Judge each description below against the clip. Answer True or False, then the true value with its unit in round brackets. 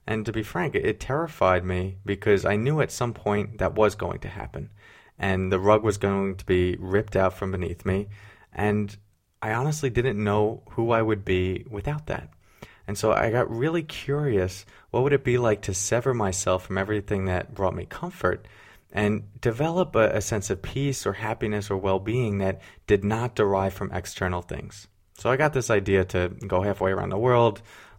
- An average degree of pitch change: True (3.2 semitones)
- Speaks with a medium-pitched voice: False (105 Hz)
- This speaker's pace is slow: False (195 wpm)